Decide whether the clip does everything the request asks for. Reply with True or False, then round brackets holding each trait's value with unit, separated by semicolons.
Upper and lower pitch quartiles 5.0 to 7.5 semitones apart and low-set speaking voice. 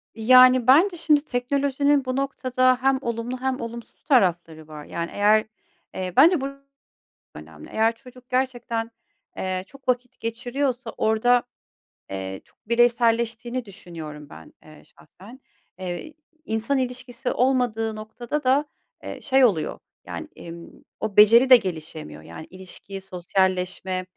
False (5.4 semitones; 235 Hz)